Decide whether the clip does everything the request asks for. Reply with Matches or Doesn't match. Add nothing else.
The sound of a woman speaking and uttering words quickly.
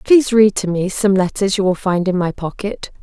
Matches